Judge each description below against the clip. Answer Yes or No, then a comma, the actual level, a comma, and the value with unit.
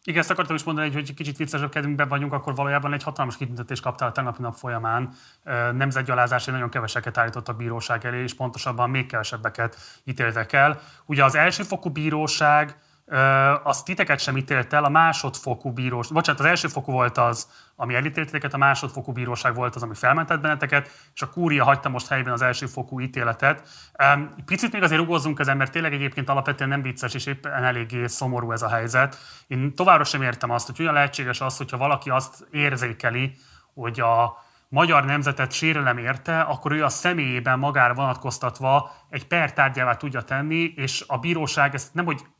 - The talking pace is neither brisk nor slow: No, fast, 175 wpm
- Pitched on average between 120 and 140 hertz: Yes, low, 135 Hz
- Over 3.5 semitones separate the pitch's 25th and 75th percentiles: No, average, 3.0 semitones